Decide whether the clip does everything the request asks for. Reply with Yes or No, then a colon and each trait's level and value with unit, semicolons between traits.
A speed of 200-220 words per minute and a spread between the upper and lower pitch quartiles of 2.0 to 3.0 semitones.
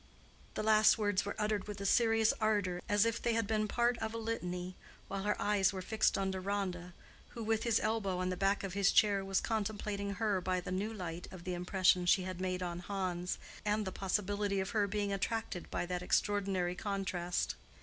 Yes: fast, 205 wpm; narrow, 2.5 semitones